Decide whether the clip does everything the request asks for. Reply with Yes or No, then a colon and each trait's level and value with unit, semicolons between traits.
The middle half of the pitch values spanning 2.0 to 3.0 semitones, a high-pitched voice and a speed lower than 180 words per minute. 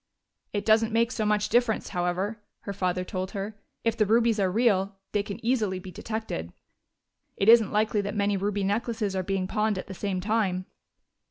No: narrow, 2.5 semitones; high, 205 Hz; average, 185 wpm